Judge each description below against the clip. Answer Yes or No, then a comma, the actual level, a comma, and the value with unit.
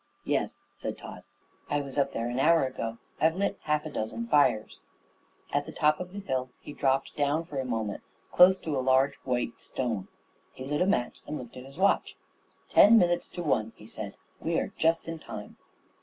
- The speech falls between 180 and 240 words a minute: Yes, average, 200 wpm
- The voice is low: No, medium, 145 Hz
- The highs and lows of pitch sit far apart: No, average, 4.6 semitones